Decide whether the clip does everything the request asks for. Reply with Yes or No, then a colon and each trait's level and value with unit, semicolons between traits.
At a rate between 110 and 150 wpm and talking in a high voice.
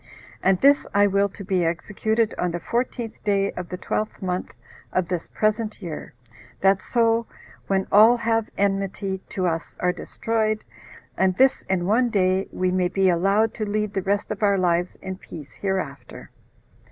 No: average, 175 wpm; high, 195 Hz